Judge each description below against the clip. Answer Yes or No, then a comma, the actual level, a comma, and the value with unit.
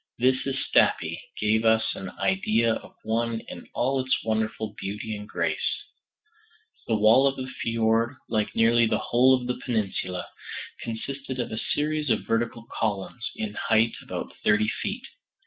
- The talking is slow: No, average, 155 wpm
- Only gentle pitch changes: Yes, narrow, 2.3 semitones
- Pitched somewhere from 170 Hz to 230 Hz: No, low, 115 Hz